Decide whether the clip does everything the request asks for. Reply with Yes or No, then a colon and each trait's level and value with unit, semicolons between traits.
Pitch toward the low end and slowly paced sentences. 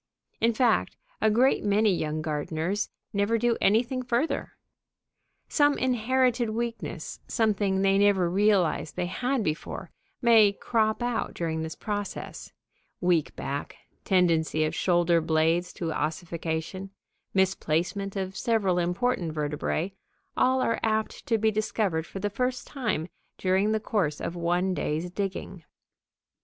No: high, 195 Hz; slow, 130 wpm